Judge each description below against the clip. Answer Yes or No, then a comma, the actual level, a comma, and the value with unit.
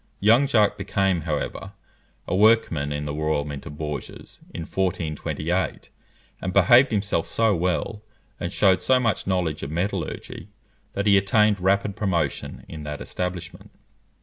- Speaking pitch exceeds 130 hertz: No, very low, 95 Hz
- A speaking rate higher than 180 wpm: No, average, 145 wpm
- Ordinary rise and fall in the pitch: Yes, average, 4.7 semitones